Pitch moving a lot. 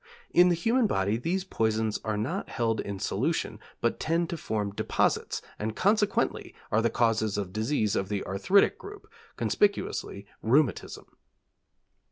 Yes: wide, 8.8 semitones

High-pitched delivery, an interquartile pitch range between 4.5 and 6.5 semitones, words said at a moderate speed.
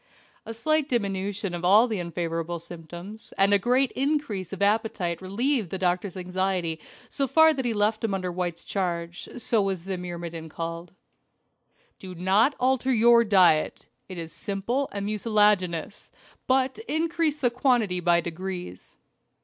Yes: high, 195 Hz; average, 5.0 semitones; average, 150 wpm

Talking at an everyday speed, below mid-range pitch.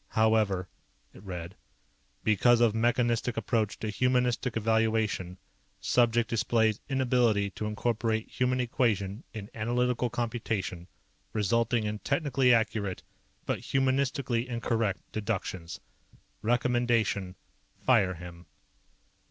No: slow, 95 wpm; low, 115 Hz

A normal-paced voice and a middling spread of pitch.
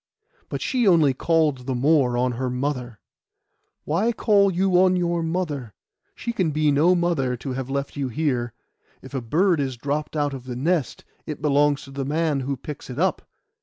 Yes: average, 185 wpm; average, 4.3 semitones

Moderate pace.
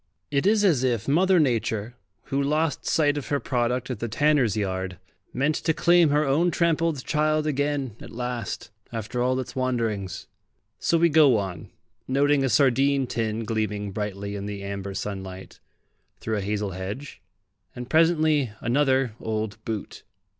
Yes: average, 155 wpm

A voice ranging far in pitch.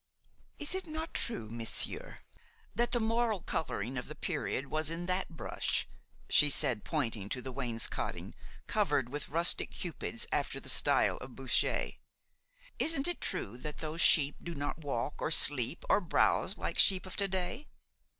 Yes: wide, 7.4 semitones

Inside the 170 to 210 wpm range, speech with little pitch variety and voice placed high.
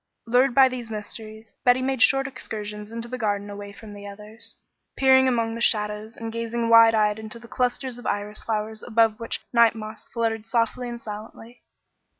Yes: average, 180 wpm; narrow, 2.0 semitones; high, 225 Hz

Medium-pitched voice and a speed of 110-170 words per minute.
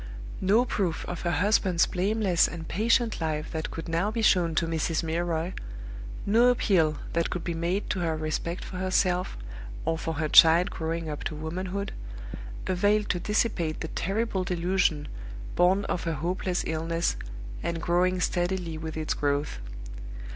Yes: medium, 175 Hz; average, 155 wpm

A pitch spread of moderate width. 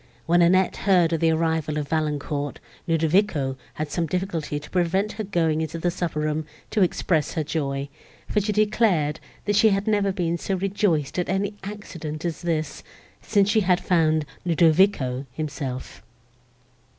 Yes: average, 4.0 semitones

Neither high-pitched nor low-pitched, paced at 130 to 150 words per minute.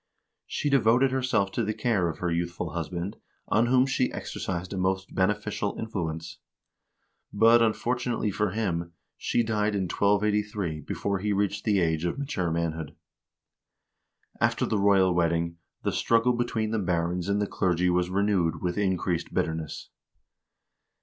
No: low, 100 Hz; average, 145 wpm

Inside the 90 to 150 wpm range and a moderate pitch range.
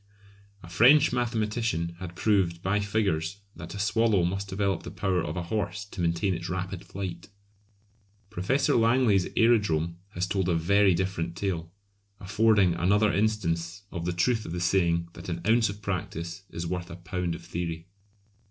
No: average, 165 wpm; average, 3.4 semitones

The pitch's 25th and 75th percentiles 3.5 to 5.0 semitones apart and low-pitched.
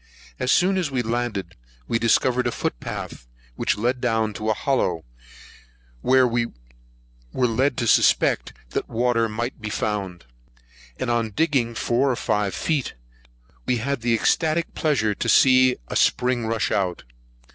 No: average, 2.8 semitones; low, 120 Hz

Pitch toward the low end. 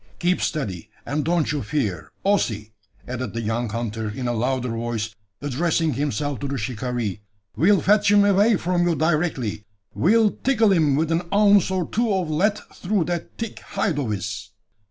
No: medium, 150 Hz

